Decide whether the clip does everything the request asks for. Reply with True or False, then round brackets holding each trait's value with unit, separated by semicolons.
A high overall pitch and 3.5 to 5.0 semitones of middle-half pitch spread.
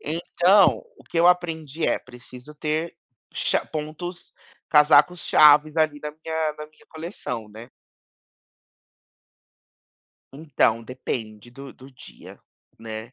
False (150 Hz; 4.1 semitones)